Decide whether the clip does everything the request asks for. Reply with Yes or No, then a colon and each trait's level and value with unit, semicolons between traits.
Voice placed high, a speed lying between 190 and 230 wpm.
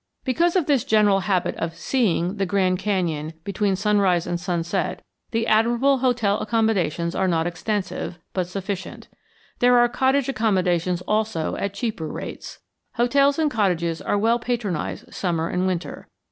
No: high, 200 Hz; average, 145 wpm